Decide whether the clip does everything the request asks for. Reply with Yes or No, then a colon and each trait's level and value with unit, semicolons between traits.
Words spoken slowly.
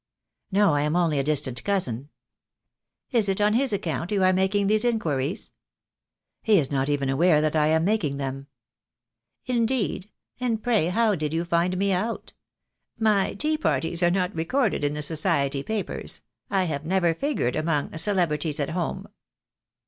No: average, 165 wpm